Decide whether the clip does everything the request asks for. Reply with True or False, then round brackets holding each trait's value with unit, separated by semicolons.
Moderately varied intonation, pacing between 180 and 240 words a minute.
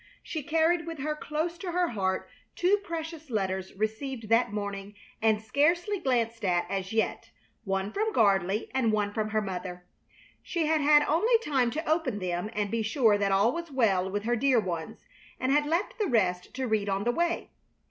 False (7.6 semitones; 190 wpm)